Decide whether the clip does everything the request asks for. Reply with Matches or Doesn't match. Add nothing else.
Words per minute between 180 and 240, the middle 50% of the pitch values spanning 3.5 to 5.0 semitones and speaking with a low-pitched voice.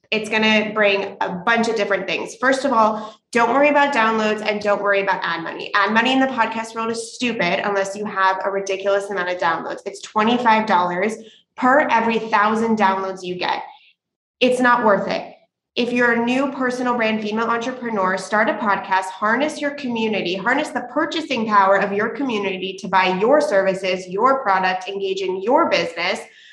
Doesn't match